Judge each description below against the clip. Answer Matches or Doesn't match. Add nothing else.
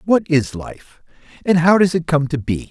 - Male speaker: Matches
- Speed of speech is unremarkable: Doesn't match